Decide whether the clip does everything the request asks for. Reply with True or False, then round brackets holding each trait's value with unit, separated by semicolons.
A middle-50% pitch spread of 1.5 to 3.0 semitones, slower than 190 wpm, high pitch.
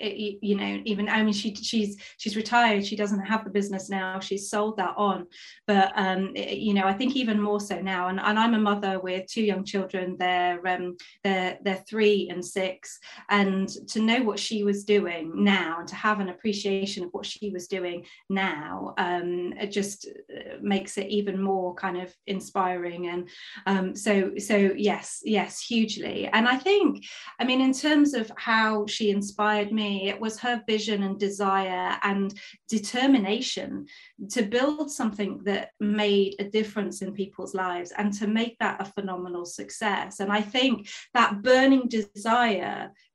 True (2.4 semitones; 175 wpm; 205 Hz)